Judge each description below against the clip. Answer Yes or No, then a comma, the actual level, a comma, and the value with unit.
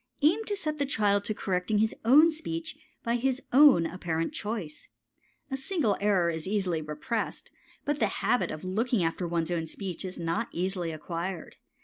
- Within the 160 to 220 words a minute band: Yes, average, 170 wpm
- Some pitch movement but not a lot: No, wide, 7.6 semitones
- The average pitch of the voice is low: No, high, 200 Hz